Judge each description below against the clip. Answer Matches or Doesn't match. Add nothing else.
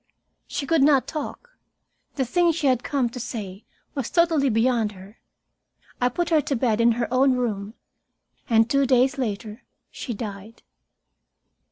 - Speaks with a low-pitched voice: Doesn't match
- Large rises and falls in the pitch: Doesn't match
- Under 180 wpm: Matches